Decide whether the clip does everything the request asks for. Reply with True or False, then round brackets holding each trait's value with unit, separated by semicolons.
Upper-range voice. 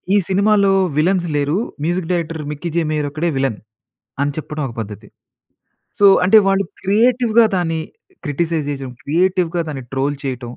False (165 Hz)